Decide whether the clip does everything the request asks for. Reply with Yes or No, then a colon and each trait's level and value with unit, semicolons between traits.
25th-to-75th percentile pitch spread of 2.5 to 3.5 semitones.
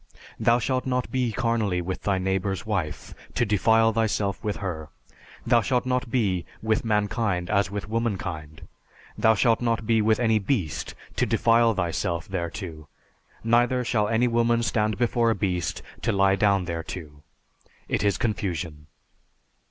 No: average, 3.9 semitones